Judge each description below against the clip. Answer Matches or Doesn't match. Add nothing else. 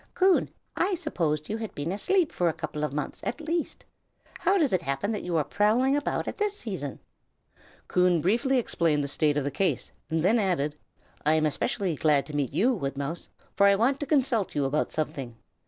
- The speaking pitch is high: Doesn't match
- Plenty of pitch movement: Matches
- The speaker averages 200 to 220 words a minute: Matches